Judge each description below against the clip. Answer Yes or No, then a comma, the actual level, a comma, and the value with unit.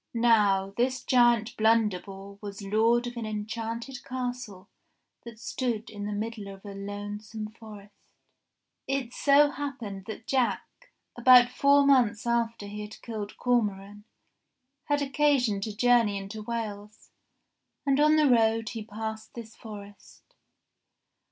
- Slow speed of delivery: Yes, slow, 130 wpm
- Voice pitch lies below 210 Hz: No, high, 225 Hz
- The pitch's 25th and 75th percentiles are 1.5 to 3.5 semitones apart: Yes, average, 2.9 semitones